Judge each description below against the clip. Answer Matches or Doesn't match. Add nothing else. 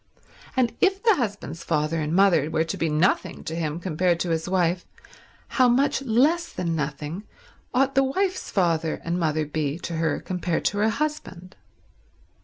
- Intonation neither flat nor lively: Doesn't match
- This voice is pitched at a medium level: Matches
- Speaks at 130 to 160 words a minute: Doesn't match